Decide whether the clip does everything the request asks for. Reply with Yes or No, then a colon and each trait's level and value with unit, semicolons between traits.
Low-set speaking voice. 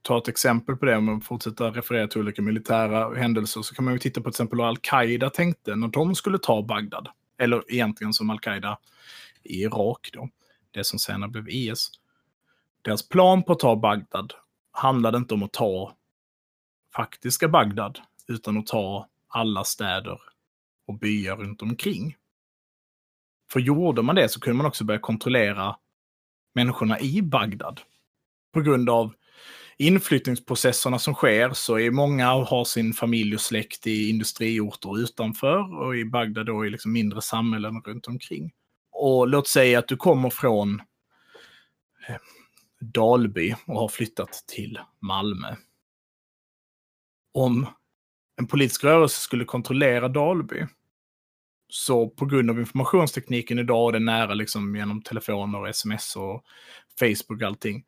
Yes: low, 115 Hz